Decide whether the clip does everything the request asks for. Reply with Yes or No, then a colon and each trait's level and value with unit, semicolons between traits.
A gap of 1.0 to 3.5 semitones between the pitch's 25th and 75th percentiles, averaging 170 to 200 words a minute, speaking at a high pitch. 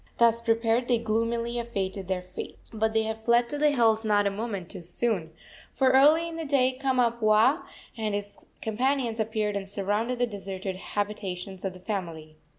Yes: average, 3.2 semitones; average, 175 wpm; high, 220 Hz